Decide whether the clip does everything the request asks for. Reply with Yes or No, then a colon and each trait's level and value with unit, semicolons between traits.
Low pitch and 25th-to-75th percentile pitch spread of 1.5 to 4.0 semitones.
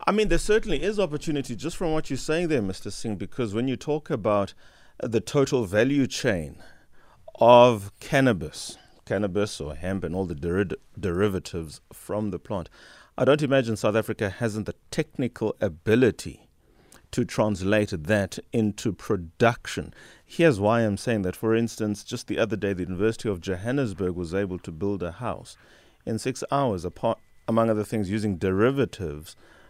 No: low, 110 Hz; average, 5.0 semitones